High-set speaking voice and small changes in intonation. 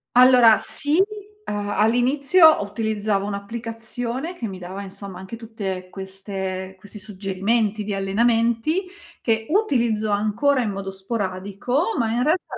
No: high, 215 Hz; average, 3.6 semitones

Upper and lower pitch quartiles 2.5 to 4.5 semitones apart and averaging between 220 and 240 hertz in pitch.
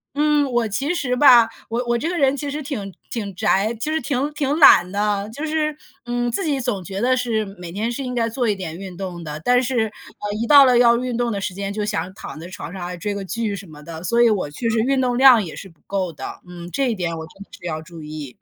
No: average, 5.2 semitones; high, 225 Hz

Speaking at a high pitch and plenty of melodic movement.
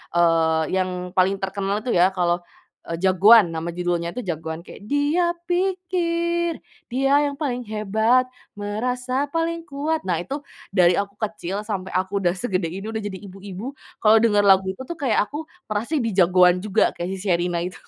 Yes: high, 205 Hz; wide, 5.9 semitones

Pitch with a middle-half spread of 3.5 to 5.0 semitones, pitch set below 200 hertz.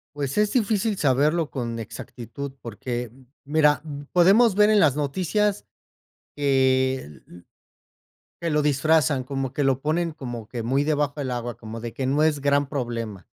Yes: average, 3.8 semitones; medium, 140 Hz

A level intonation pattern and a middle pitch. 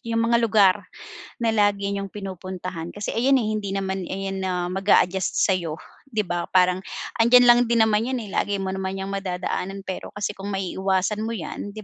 No: narrow, 2.3 semitones; high, 195 Hz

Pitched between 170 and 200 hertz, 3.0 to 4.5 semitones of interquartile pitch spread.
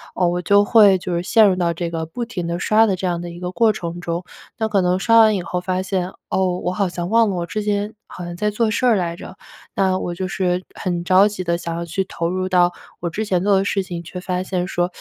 No: medium, 185 Hz; narrow, 2.5 semitones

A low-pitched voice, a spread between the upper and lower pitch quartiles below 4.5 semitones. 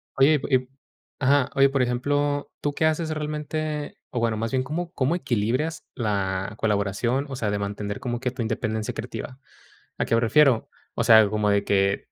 No: low, 125 Hz; average, 5.1 semitones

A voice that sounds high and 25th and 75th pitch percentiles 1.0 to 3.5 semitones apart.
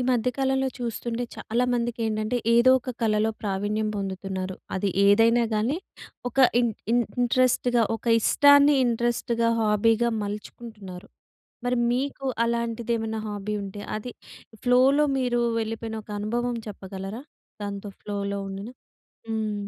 Yes: high, 225 Hz; average, 2.8 semitones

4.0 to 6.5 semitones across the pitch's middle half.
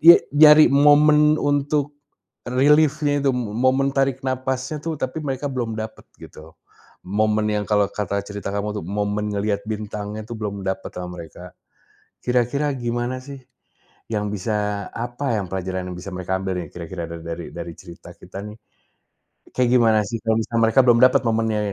Yes: average, 4.7 semitones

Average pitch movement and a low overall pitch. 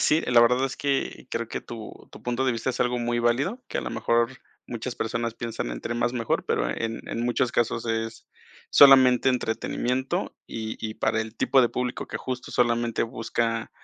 No: narrow, 1.7 semitones; low, 120 Hz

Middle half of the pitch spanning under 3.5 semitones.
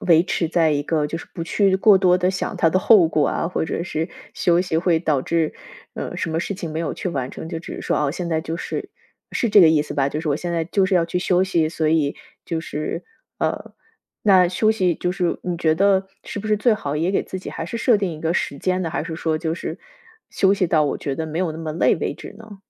Yes: average, 2.7 semitones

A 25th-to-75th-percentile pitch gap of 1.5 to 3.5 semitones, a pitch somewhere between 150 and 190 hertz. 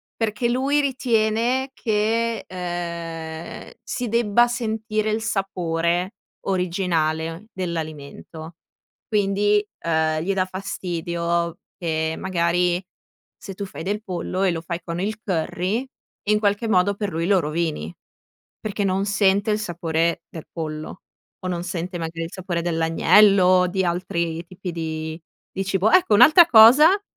No: average, 4.0 semitones; medium, 185 Hz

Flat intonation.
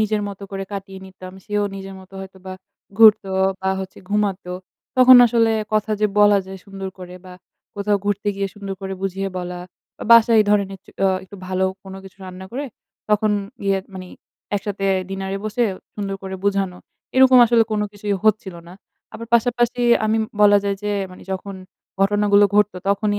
Yes: narrow, 1.6 semitones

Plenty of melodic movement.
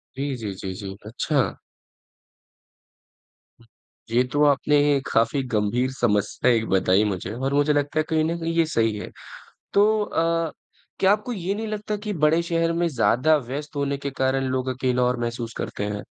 Yes: wide, 5.8 semitones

